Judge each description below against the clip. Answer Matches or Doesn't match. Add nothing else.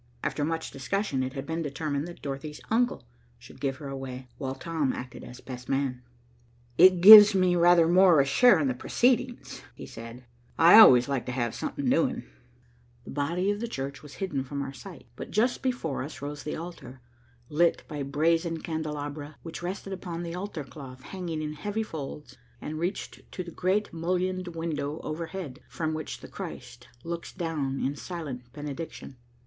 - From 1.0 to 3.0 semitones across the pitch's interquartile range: Doesn't match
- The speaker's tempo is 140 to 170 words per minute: Doesn't match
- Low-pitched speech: Doesn't match